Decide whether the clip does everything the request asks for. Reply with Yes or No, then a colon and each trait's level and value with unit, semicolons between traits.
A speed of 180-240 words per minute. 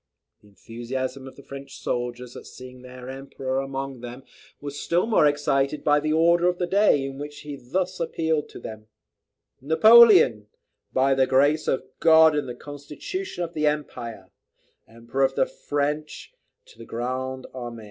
No: average, 170 wpm